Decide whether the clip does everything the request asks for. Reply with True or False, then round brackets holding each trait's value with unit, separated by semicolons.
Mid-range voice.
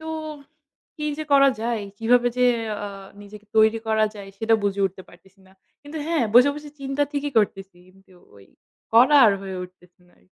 False (220 Hz)